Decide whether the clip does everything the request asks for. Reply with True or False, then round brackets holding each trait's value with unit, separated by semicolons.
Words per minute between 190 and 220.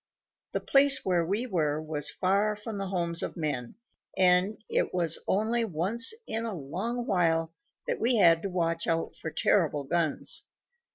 False (165 wpm)